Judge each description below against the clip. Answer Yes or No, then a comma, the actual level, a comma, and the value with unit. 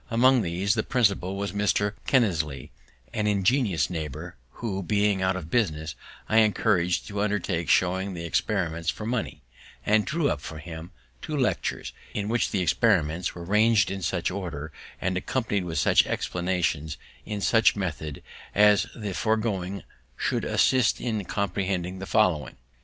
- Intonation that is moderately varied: Yes, average, 3.7 semitones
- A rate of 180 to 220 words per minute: No, average, 150 wpm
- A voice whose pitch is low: Yes, very low, 95 Hz